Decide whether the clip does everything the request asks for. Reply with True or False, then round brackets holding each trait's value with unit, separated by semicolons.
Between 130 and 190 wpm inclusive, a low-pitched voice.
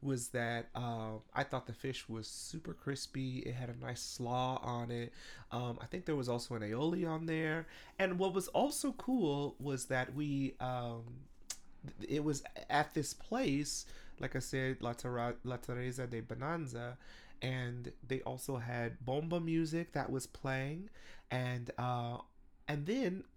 True (165 wpm; 130 Hz)